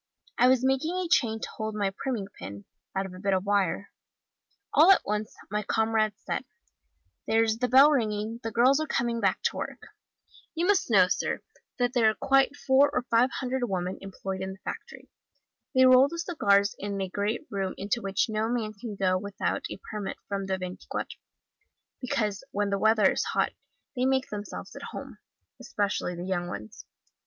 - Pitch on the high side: Yes, high, 215 Hz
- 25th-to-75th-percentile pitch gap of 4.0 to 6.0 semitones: Yes, average, 4.4 semitones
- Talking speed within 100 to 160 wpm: No, average, 185 wpm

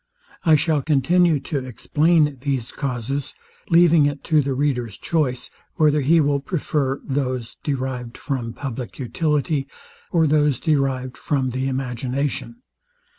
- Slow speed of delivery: Yes, slow, 125 wpm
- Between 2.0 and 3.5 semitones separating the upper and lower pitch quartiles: Yes, average, 2.8 semitones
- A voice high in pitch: No, medium, 140 Hz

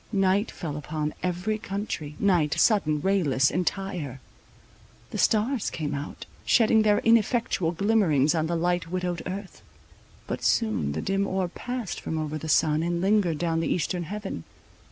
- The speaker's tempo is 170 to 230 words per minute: No, average, 155 wpm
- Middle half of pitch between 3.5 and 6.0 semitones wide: Yes, average, 4.6 semitones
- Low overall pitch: No, medium, 180 Hz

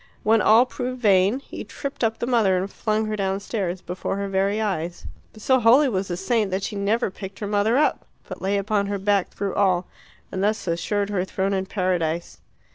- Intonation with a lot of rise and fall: No, narrow, 2.5 semitones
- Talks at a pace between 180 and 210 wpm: Yes, fast, 205 wpm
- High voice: Yes, high, 200 Hz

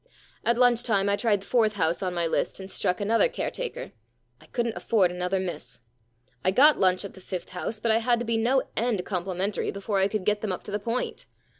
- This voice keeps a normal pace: No, fast, 240 wpm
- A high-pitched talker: Yes, high, 205 Hz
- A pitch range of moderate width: Yes, average, 3.7 semitones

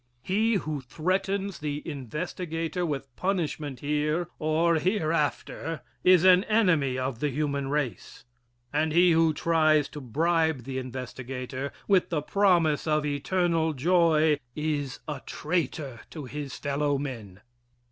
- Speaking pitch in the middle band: Yes, medium, 155 Hz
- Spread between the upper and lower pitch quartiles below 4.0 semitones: Yes, average, 3.3 semitones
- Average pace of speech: No, slow, 125 wpm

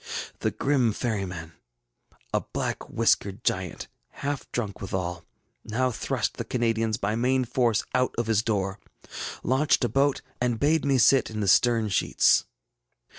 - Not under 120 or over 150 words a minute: Yes, average, 145 wpm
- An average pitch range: Yes, average, 4.2 semitones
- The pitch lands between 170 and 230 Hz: No, low, 115 Hz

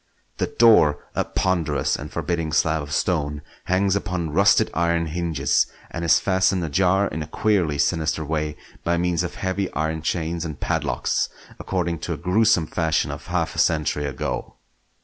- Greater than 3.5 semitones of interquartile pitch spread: No, average, 3.0 semitones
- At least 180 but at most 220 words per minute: No, average, 165 wpm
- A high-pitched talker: No, very low, 85 Hz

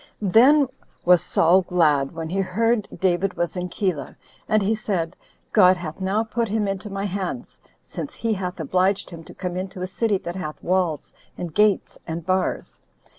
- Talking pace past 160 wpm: Yes, average, 175 wpm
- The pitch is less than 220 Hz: Yes, medium, 185 Hz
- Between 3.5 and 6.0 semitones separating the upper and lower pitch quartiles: No, average, 2.9 semitones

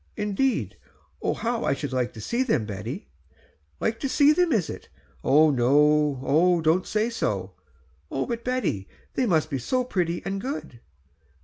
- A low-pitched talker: No, medium, 175 Hz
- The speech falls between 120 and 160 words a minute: Yes, average, 155 wpm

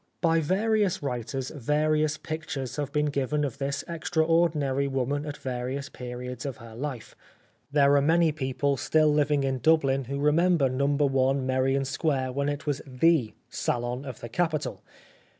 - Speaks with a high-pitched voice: No, medium, 140 Hz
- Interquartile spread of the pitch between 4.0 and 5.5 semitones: No, average, 2.7 semitones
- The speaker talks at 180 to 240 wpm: No, average, 155 wpm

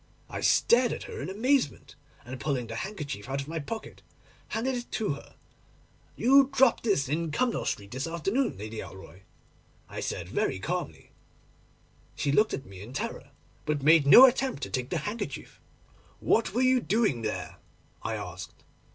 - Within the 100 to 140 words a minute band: No, average, 170 wpm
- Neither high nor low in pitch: Yes, medium, 165 Hz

